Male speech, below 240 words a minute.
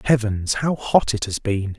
Yes: male; average, 200 wpm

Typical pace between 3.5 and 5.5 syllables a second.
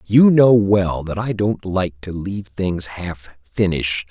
Yes: 4.0 syllables/s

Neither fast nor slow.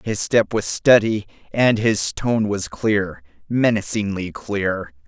No: slow, 130 wpm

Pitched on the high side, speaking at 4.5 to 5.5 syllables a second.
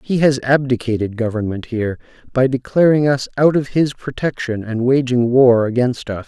No: low, 125 Hz; 5.1 syllables/s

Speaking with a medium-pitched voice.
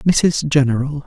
Yes: medium, 145 Hz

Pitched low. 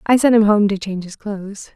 No: high, 205 Hz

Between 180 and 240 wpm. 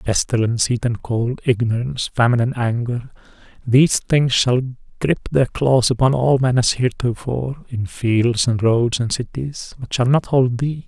No: average, 165 wpm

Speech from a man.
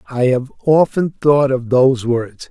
Yes: male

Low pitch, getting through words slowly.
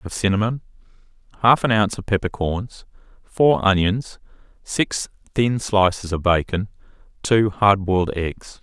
Yes: low, 100 Hz; slow, 125 wpm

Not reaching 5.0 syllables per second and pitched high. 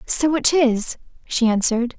Yes: 4.4 syllables/s; very high, 255 Hz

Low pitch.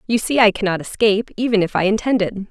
No: high, 210 Hz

